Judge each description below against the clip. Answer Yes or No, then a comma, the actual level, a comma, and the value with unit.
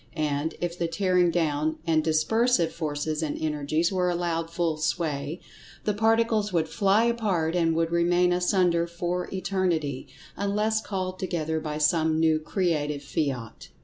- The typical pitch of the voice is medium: Yes, medium, 170 Hz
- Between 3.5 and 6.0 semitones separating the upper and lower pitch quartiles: No, average, 2.9 semitones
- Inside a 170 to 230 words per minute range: No, average, 145 wpm